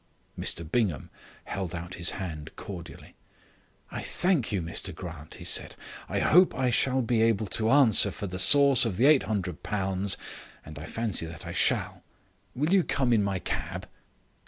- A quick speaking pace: No, average, 165 wpm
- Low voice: Yes, low, 100 Hz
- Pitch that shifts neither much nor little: No, wide, 5.9 semitones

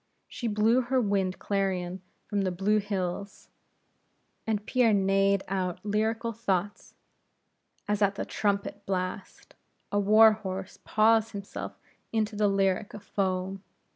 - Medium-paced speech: No, slow, 130 wpm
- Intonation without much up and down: Yes, narrow, 1.9 semitones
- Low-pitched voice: No, high, 200 Hz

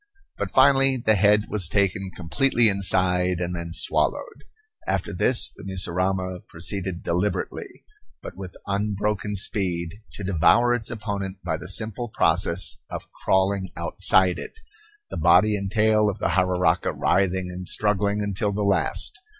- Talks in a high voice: No, very low, 95 Hz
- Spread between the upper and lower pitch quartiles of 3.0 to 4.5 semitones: No, narrow, 2.5 semitones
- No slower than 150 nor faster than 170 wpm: No, average, 140 wpm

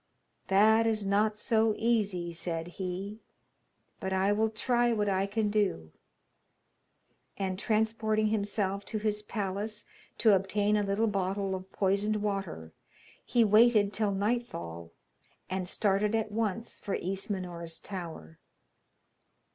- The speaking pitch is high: Yes, high, 205 Hz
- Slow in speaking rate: Yes, slow, 125 wpm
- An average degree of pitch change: No, narrow, 2.3 semitones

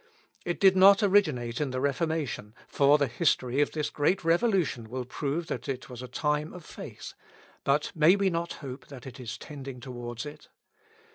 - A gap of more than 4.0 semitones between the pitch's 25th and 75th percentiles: Yes, average, 4.7 semitones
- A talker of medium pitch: Yes, medium, 145 Hz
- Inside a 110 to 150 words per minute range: No, average, 185 wpm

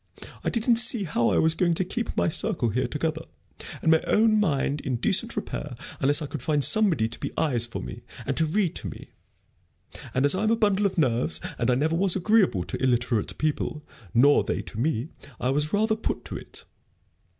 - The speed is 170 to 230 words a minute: Yes, fast, 205 wpm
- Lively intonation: Yes, wide, 7.3 semitones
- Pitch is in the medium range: Yes, medium, 155 Hz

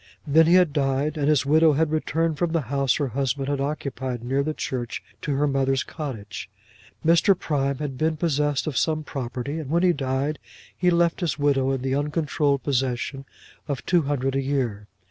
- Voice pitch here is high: No, medium, 140 Hz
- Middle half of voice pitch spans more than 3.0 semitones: No, narrow, 2.6 semitones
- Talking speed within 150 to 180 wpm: No, average, 190 wpm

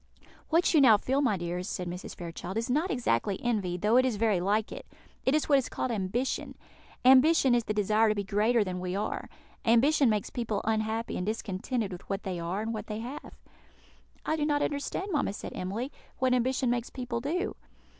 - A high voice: Yes, high, 225 Hz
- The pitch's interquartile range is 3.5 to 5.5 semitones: Yes, average, 4.6 semitones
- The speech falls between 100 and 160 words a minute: No, fast, 205 wpm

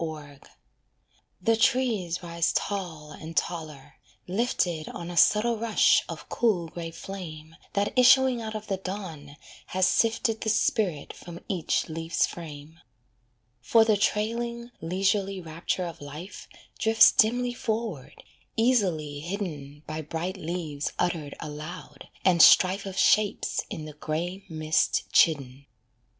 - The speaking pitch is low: No, medium, 175 Hz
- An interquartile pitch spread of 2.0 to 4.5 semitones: No, average, 5.2 semitones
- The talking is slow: Yes, slow, 130 wpm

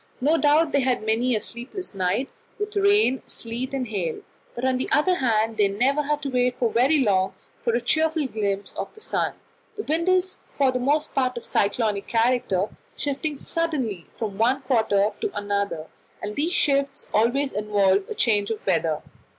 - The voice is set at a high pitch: Yes, very high, 250 Hz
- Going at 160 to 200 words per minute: Yes, average, 180 wpm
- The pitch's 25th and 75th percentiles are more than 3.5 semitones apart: Yes, wide, 5.5 semitones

